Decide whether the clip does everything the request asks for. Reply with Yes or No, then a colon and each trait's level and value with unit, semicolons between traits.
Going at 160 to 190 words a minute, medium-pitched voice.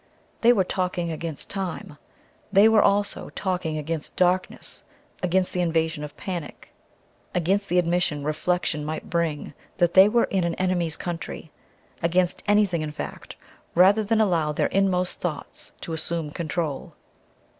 No: average, 145 wpm; medium, 175 Hz